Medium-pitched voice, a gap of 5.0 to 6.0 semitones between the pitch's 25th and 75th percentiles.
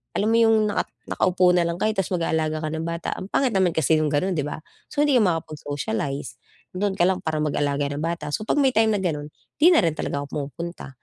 No: medium, 170 Hz; average, 4.4 semitones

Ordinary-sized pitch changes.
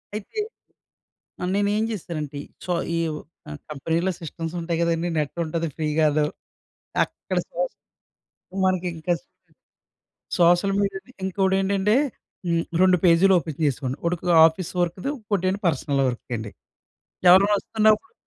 Yes: average, 3.1 semitones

